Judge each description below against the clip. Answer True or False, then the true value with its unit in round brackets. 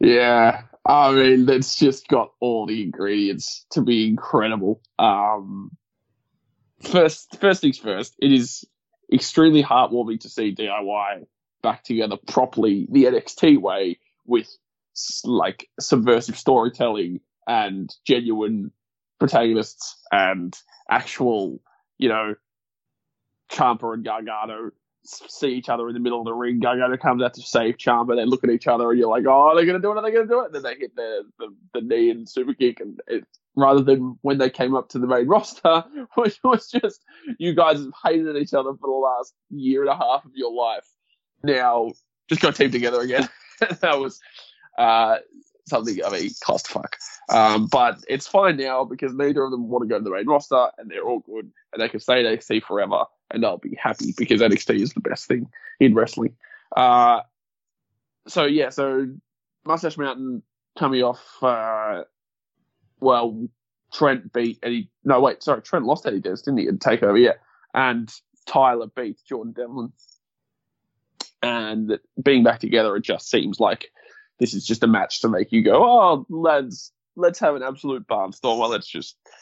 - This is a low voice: True (130 Hz)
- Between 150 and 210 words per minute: True (175 wpm)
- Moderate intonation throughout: False (5.9 semitones)